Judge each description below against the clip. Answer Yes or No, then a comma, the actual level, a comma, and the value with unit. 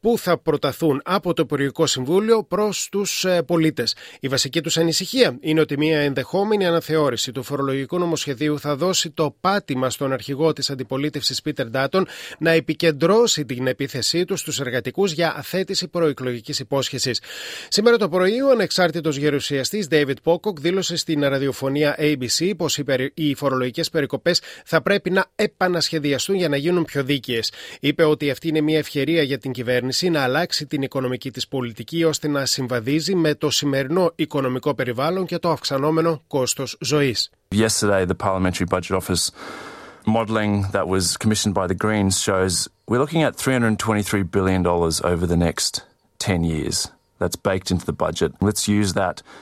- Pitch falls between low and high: Yes, medium, 145 Hz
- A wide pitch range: No, average, 4.7 semitones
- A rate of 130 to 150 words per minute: No, slow, 115 wpm